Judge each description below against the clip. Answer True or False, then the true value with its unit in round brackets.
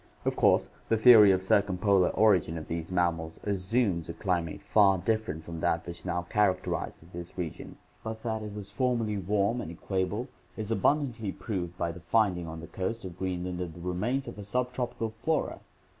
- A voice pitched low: True (95 Hz)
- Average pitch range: True (4.0 semitones)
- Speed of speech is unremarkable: True (190 wpm)